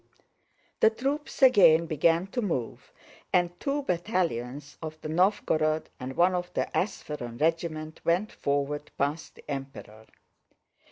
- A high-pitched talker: No, medium, 160 Hz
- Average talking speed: No, slow, 125 wpm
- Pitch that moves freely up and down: No, average, 4.2 semitones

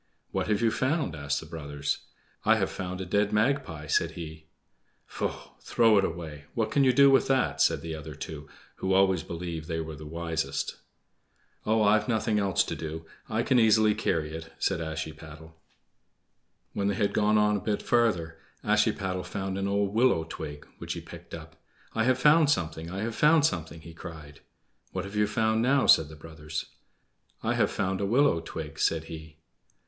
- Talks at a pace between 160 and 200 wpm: Yes, average, 185 wpm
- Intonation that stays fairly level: No, wide, 5.4 semitones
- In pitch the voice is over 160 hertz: No, very low, 95 Hz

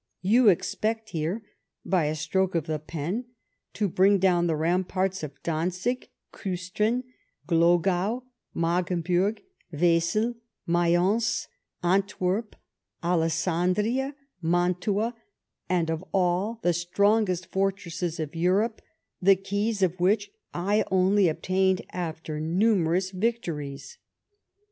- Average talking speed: No, slow, 100 wpm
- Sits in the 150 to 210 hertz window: Yes, medium, 185 Hz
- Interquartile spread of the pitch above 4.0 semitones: No, average, 3.1 semitones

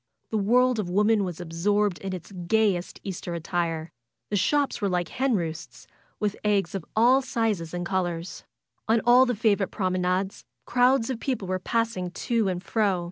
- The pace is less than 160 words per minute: No, average, 175 wpm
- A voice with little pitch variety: No, average, 4.2 semitones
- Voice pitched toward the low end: No, high, 195 Hz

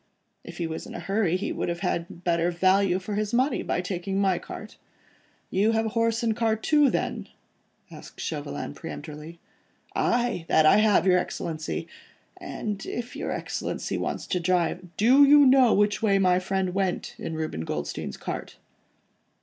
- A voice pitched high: Yes, high, 195 Hz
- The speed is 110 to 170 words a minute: No, average, 180 wpm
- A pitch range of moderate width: Yes, average, 4.3 semitones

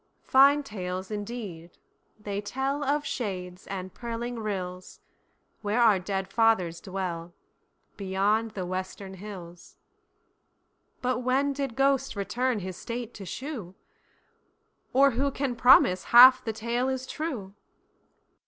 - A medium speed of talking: No, slow, 105 wpm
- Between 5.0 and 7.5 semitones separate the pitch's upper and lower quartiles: Yes, average, 5.3 semitones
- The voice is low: No, high, 215 Hz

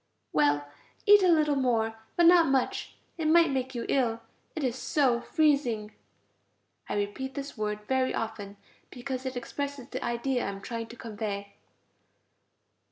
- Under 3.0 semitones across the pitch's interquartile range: No, average, 4.2 semitones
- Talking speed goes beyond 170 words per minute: No, average, 155 wpm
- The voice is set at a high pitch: Yes, very high, 255 Hz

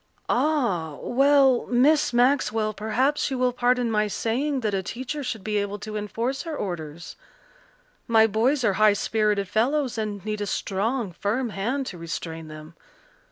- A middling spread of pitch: Yes, average, 4.1 semitones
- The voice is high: Yes, high, 220 Hz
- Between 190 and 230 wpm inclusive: No, average, 160 wpm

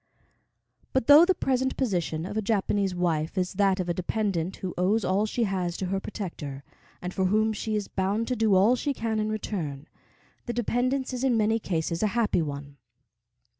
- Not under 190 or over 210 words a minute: Yes, average, 195 wpm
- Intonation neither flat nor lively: Yes, average, 3.9 semitones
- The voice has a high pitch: Yes, high, 200 Hz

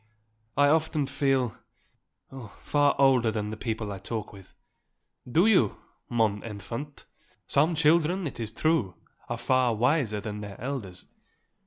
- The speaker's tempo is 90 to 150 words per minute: Yes, average, 140 wpm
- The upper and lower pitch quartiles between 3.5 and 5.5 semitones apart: Yes, average, 5.2 semitones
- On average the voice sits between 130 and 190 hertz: No, low, 120 Hz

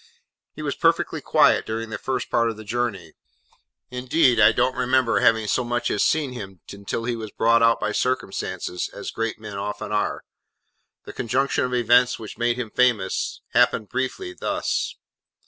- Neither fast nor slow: Yes, average, 170 wpm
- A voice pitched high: No, low, 115 Hz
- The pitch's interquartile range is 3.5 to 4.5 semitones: No, average, 2.9 semitones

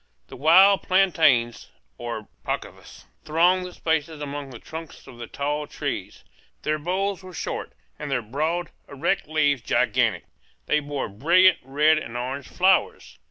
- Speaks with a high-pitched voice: No, medium, 150 Hz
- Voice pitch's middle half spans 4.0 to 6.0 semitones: Yes, average, 4.4 semitones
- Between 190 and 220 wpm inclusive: No, average, 145 wpm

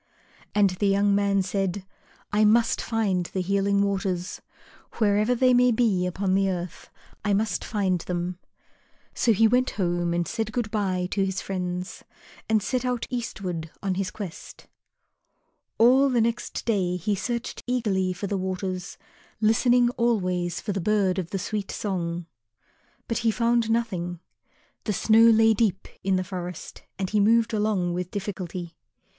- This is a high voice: Yes, high, 200 Hz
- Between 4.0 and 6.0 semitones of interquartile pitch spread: No, average, 3.4 semitones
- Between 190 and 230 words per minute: No, average, 155 wpm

